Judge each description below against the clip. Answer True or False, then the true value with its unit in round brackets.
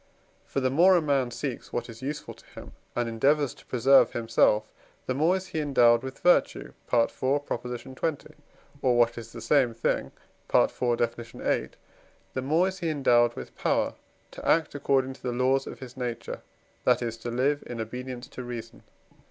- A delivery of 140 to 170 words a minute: False (185 wpm)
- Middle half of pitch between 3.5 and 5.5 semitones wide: False (3.1 semitones)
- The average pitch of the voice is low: True (130 Hz)